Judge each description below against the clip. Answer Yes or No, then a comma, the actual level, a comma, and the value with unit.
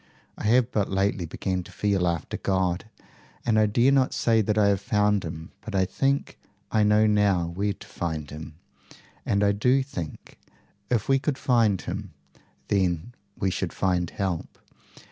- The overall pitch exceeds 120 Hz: No, low, 100 Hz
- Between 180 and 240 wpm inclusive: No, average, 170 wpm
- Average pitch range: Yes, average, 3.4 semitones